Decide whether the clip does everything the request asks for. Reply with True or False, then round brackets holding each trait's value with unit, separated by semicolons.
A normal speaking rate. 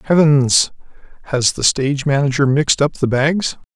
True (145 wpm)